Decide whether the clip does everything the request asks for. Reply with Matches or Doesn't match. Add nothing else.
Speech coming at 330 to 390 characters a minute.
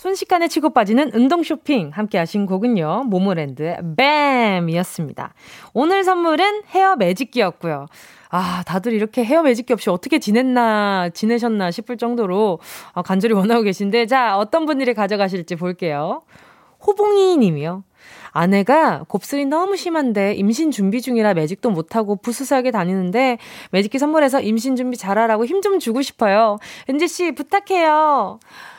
Matches